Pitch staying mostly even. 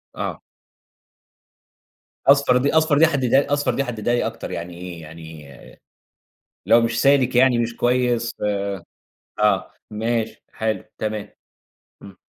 No: average, 3.9 semitones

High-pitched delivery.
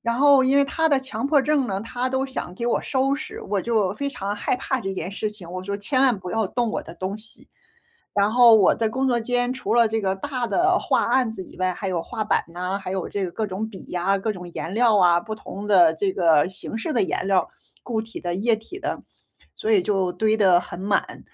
Yes: high, 215 Hz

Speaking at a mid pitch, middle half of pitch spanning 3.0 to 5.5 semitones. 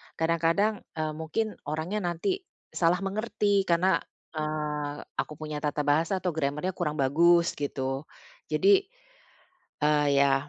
Yes: medium, 160 Hz; average, 3.9 semitones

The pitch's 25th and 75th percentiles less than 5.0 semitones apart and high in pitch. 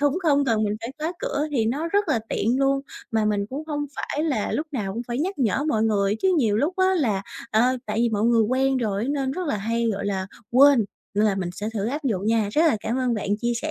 No: wide, 5.4 semitones; high, 240 Hz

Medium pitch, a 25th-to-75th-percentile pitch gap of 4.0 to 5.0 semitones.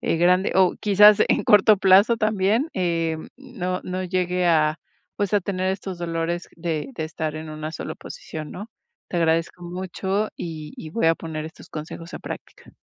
No: medium, 180 Hz; average, 2.9 semitones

